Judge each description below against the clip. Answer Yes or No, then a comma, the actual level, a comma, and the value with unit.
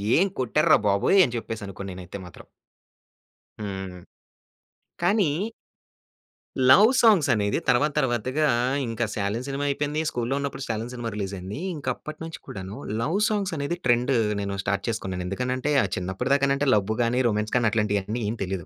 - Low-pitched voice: Yes, low, 120 Hz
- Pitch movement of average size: No, wide, 6.0 semitones